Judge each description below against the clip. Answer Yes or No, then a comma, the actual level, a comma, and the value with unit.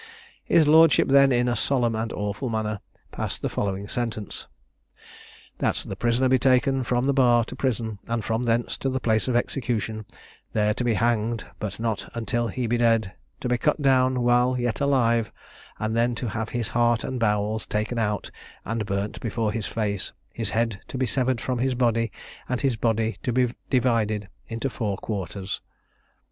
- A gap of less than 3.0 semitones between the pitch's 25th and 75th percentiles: Yes, narrow, 2.5 semitones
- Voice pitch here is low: Yes, low, 115 Hz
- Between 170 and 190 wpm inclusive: Yes, average, 180 wpm